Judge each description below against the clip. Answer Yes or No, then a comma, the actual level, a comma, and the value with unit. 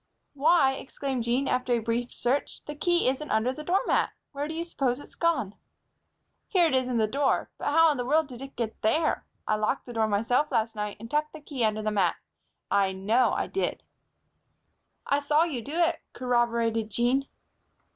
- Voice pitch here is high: Yes, very high, 255 Hz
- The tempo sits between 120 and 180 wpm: No, average, 195 wpm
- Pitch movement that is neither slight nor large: Yes, average, 4.6 semitones